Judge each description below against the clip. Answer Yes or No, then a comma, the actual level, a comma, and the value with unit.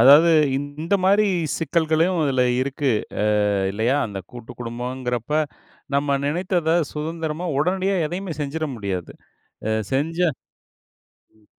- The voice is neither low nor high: Yes, medium, 150 Hz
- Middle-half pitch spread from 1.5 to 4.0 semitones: No, average, 4.8 semitones